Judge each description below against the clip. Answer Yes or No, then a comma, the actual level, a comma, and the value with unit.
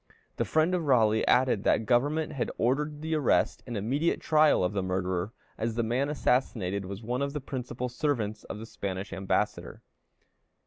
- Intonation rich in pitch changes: Yes, wide, 5.7 semitones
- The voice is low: Yes, low, 120 Hz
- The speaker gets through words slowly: No, average, 175 wpm